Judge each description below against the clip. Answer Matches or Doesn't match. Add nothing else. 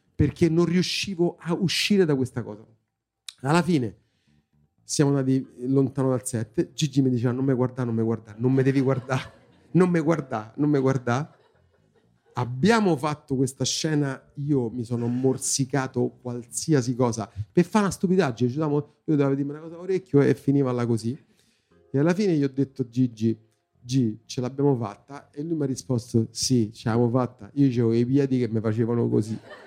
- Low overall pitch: Matches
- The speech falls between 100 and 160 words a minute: Doesn't match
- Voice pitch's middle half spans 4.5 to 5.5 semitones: Doesn't match